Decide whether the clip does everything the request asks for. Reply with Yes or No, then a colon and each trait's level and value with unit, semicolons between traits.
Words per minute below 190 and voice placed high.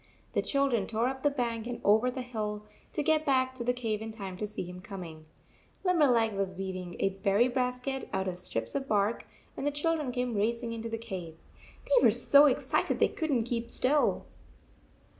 No: fast, 205 wpm; high, 235 Hz